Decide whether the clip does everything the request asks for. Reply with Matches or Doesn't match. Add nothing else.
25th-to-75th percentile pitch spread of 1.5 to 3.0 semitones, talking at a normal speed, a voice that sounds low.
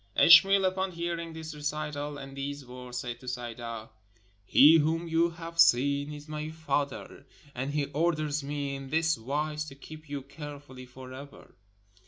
Doesn't match